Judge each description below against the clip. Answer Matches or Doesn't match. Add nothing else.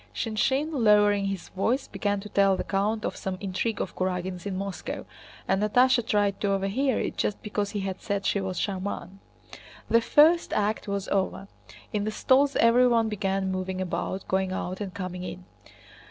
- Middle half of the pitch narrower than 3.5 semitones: Matches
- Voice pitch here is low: Doesn't match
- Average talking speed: Matches